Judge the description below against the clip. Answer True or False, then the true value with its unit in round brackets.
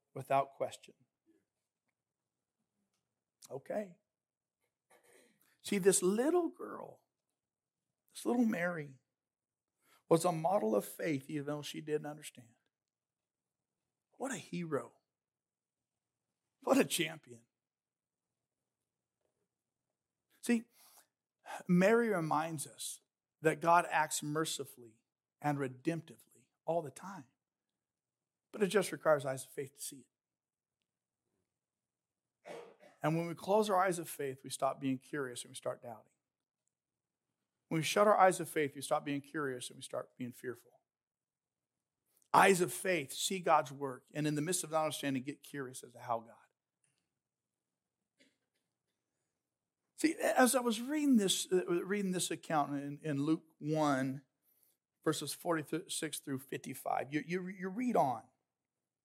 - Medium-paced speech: False (125 wpm)